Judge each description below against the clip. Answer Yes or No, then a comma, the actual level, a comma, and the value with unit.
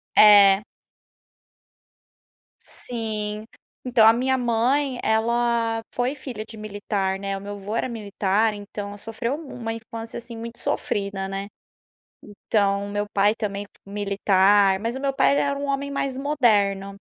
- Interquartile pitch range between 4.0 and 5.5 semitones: No, average, 3.0 semitones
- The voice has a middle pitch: No, high, 220 Hz